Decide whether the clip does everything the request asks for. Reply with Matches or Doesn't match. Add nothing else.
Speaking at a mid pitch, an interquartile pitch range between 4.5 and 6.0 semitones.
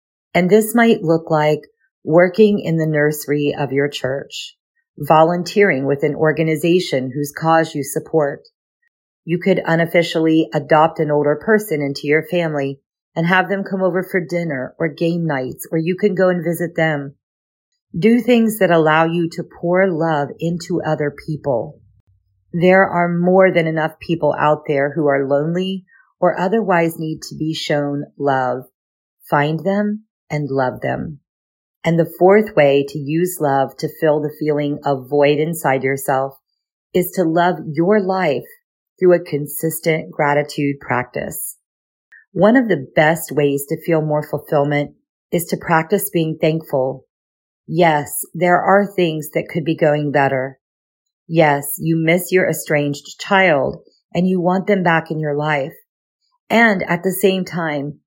Doesn't match